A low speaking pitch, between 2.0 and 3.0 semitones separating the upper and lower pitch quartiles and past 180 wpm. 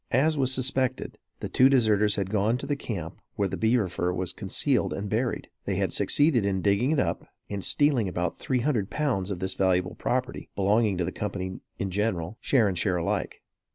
No: low, 105 Hz; average, 5.3 semitones; average, 200 wpm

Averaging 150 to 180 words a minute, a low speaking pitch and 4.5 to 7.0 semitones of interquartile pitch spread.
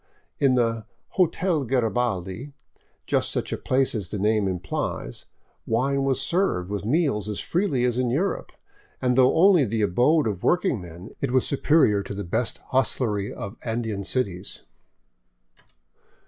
Yes: average, 160 wpm; low, 120 Hz; average, 5.0 semitones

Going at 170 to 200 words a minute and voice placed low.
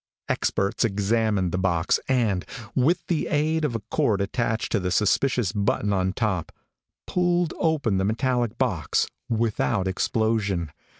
No: slow, 135 wpm; low, 110 Hz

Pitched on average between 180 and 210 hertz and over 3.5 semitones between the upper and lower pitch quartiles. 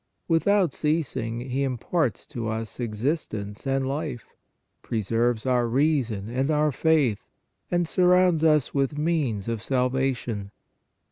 No: low, 130 Hz; average, 5.0 semitones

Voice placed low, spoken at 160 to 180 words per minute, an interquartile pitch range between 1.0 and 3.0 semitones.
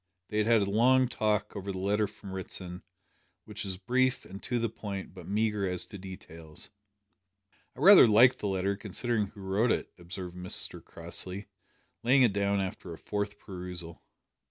Yes: low, 100 Hz; average, 175 wpm; average, 2.7 semitones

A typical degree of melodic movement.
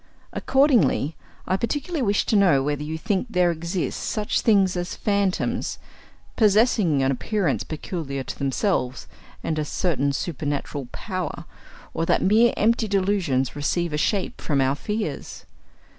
No: wide, 6.2 semitones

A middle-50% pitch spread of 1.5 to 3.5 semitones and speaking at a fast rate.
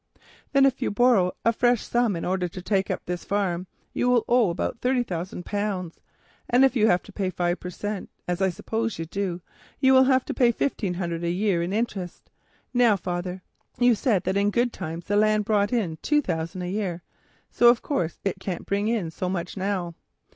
No: average, 4.9 semitones; fast, 210 wpm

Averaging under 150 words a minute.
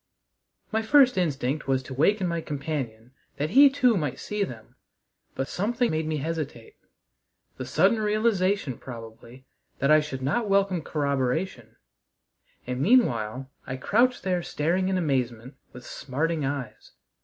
Yes: average, 140 wpm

